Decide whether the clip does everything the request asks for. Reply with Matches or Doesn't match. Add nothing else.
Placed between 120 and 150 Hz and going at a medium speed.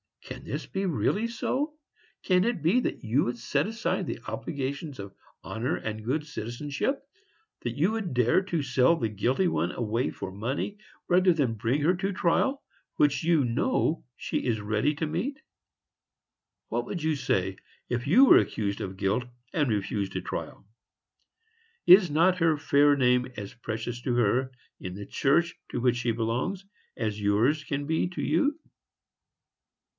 Matches